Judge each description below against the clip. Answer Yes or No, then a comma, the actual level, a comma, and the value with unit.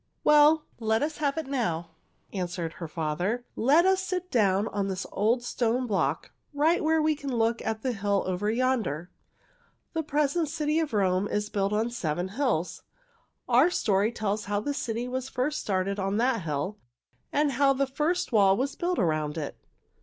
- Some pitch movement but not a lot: No, wide, 6.6 semitones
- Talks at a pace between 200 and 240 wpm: No, average, 175 wpm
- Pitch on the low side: No, high, 230 Hz